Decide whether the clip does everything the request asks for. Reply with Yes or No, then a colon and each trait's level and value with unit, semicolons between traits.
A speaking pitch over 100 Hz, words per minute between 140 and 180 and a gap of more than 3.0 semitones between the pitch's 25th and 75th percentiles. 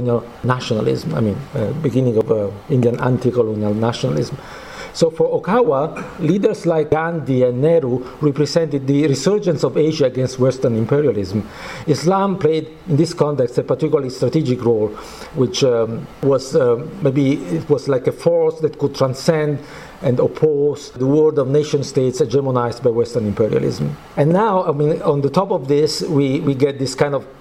Yes: medium, 140 Hz; average, 160 wpm; average, 3.7 semitones